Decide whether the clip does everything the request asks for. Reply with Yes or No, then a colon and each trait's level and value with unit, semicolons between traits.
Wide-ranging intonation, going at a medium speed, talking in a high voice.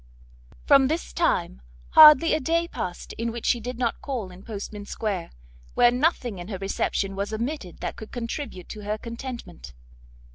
No: average, 4.9 semitones; average, 170 wpm; high, 230 Hz